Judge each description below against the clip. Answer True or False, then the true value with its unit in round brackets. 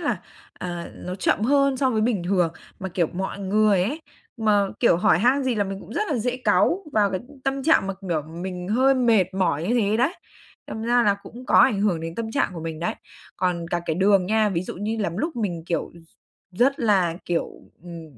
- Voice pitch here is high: True (200 Hz)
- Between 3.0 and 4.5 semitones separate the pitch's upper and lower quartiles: False (5.1 semitones)